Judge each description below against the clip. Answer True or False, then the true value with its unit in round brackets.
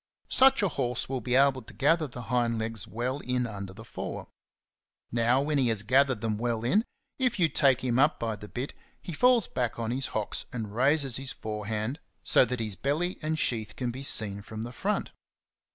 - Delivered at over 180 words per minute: True (205 wpm)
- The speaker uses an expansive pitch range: False (3.9 semitones)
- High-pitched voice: False (125 Hz)